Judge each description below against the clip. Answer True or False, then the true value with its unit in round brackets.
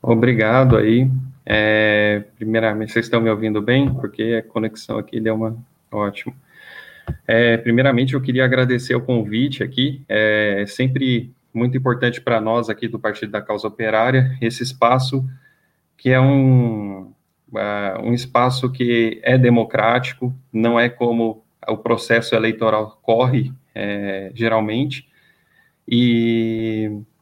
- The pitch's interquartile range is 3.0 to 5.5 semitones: False (2.6 semitones)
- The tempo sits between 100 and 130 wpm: True (125 wpm)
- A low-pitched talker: True (115 Hz)